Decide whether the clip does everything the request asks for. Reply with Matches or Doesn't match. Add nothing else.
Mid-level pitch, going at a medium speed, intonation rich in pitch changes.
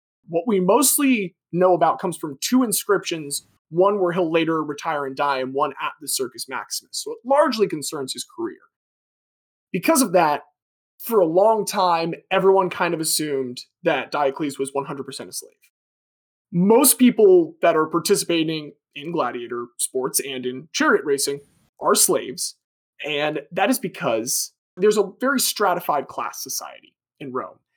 Matches